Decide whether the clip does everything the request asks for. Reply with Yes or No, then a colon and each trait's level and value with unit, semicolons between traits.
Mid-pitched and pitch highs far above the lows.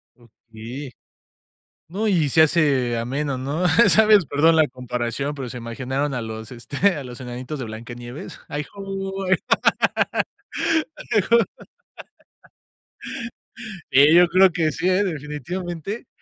Yes: medium, 145 Hz; wide, 6.3 semitones